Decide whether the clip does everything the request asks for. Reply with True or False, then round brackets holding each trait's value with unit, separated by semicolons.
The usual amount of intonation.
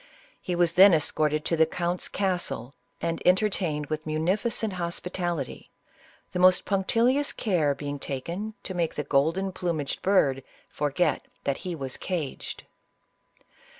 True (3.9 semitones)